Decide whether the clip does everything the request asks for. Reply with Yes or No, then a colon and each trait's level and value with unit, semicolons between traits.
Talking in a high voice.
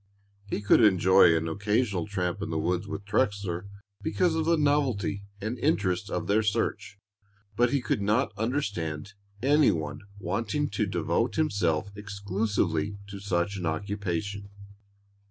No: low, 100 Hz